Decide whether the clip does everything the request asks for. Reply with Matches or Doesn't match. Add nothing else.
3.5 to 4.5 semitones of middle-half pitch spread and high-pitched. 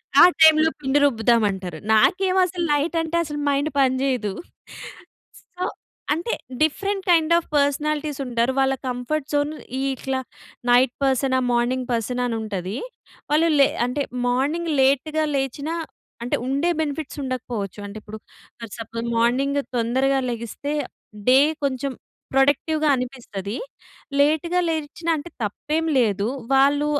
Matches